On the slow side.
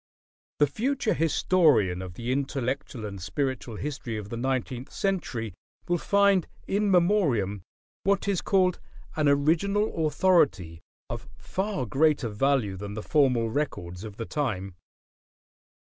Yes: slow, 130 wpm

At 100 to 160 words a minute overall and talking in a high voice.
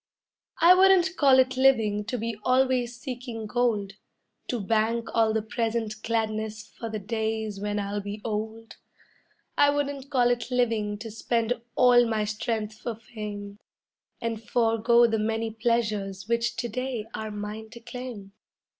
Yes: average, 150 wpm; high, 225 Hz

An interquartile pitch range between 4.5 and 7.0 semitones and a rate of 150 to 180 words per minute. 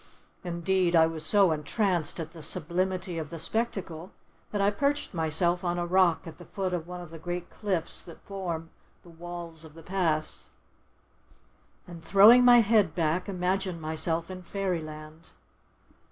No: average, 2.7 semitones; average, 160 wpm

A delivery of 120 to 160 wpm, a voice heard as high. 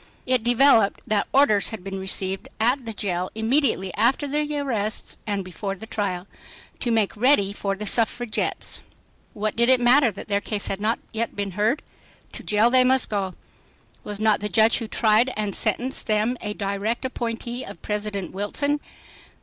No: average, 175 wpm; high, 215 Hz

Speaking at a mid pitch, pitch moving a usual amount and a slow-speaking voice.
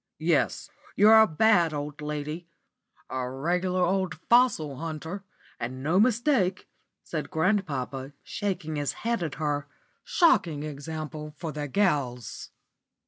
Yes: medium, 160 Hz; average, 4.7 semitones; slow, 120 wpm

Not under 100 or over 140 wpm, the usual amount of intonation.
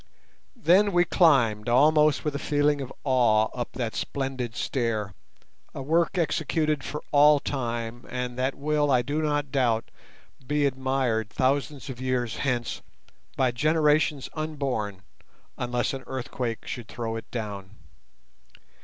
Yes: slow, 135 wpm; average, 3.7 semitones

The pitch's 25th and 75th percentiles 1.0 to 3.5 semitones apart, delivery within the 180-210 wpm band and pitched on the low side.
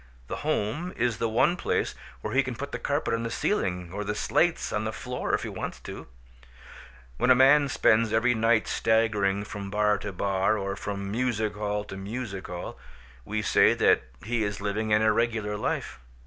Yes: average, 2.7 semitones; average, 190 wpm; low, 110 Hz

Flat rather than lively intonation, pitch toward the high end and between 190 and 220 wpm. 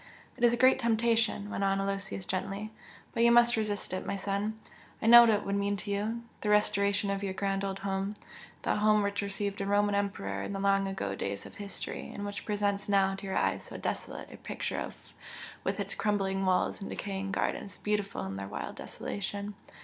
Yes: narrow, 1.2 semitones; high, 200 Hz; fast, 205 wpm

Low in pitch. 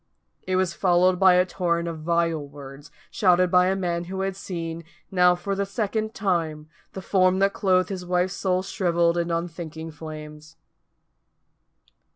No: medium, 180 Hz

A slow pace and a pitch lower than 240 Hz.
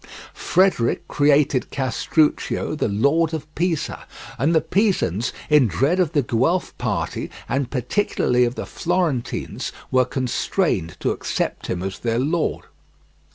Yes: slow, 130 wpm; medium, 140 Hz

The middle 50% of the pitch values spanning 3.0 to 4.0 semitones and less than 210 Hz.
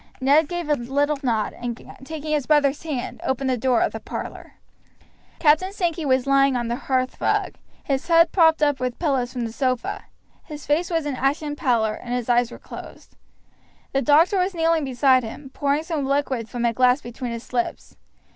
No: average, 3.6 semitones; very high, 275 Hz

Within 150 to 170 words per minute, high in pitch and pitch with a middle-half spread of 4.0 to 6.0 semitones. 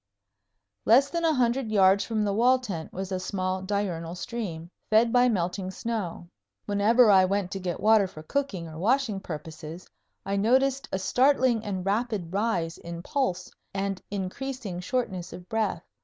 Yes: average, 160 wpm; high, 200 Hz; average, 4.4 semitones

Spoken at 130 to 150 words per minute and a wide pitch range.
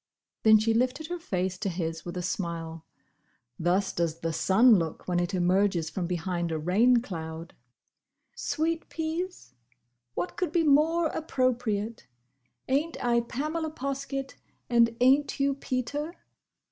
Yes: slow, 135 wpm; wide, 8.0 semitones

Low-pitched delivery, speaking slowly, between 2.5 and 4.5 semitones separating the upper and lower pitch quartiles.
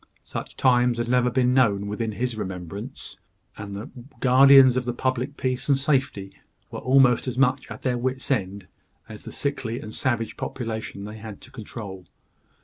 No: low, 120 Hz; average, 170 wpm; average, 3.5 semitones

